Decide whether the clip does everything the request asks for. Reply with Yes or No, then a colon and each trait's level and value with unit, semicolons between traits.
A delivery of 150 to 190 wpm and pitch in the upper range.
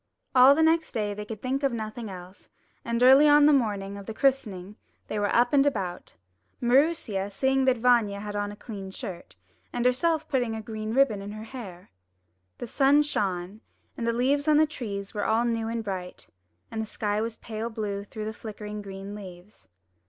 No: average, 200 wpm; high, 220 Hz